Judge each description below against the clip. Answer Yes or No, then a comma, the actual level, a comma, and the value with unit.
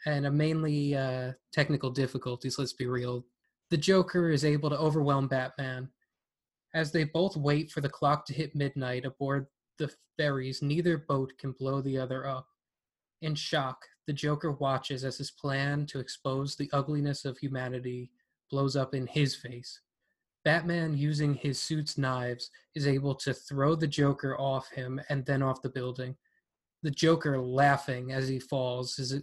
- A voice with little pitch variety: Yes, narrow, 2.2 semitones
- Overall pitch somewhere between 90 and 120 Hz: No, medium, 140 Hz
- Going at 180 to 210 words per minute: No, average, 165 wpm